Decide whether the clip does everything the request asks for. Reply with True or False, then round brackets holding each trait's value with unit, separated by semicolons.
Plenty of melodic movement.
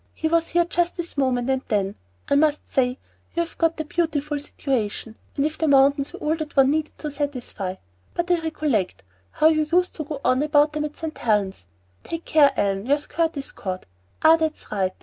False (3.9 semitones)